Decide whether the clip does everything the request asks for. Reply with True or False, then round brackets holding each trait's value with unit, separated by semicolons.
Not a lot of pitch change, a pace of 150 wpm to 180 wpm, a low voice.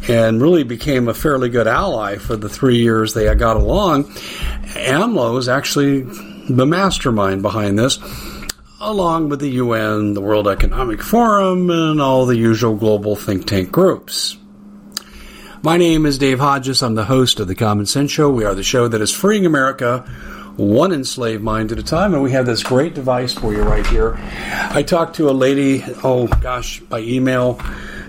False (4.7 semitones; 175 wpm; 125 Hz)